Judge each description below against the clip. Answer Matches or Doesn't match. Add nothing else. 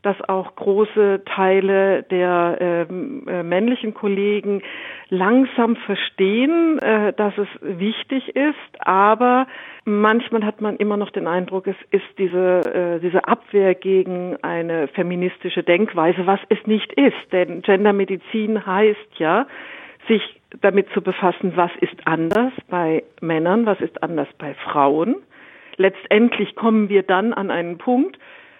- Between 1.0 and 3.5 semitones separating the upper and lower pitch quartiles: Matches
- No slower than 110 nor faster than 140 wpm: Matches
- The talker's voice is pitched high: Matches